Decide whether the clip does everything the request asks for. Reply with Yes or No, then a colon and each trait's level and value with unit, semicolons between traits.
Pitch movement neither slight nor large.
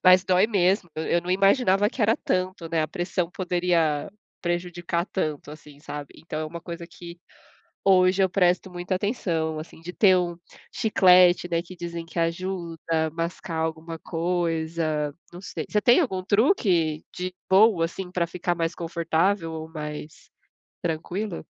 No: narrow, 2.1 semitones